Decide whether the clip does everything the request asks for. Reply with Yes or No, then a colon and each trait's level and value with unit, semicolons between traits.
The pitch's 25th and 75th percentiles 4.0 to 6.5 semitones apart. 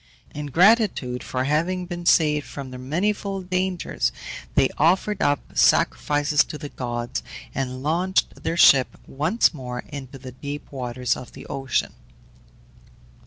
Yes: wide, 5.5 semitones